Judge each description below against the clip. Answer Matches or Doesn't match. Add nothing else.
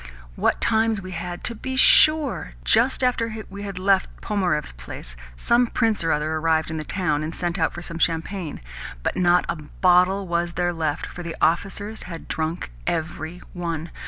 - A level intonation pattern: Doesn't match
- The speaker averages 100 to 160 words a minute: Doesn't match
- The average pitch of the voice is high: Doesn't match